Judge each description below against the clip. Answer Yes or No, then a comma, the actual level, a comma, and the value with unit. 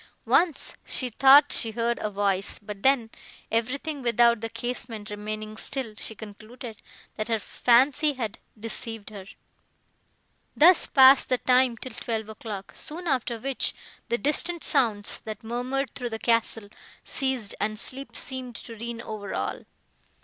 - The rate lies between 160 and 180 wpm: No, average, 145 wpm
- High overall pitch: Yes, high, 235 Hz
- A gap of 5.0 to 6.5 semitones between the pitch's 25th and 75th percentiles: No, average, 3.4 semitones